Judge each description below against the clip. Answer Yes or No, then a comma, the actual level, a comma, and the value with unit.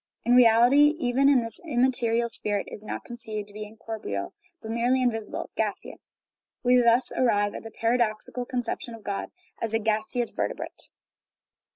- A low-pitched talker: No, high, 230 Hz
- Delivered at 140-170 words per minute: Yes, average, 155 wpm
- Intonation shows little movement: Yes, narrow, 2.3 semitones